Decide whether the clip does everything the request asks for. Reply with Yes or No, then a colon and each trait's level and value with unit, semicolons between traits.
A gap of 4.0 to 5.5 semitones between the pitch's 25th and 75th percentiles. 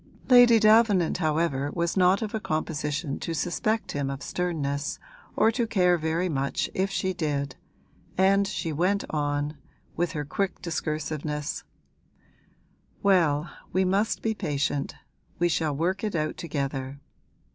Yes: average, 4.6 semitones